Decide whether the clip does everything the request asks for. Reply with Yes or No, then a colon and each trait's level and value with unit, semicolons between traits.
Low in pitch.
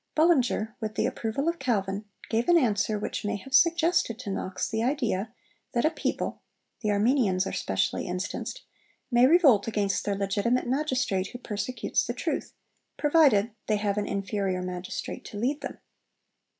No: high, 220 Hz